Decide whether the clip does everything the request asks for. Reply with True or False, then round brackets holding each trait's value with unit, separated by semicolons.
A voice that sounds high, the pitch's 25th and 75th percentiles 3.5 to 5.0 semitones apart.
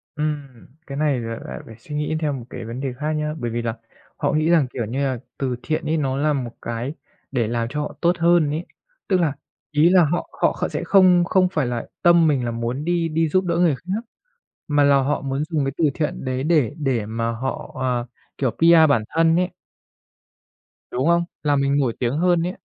False (145 Hz; 4.5 semitones)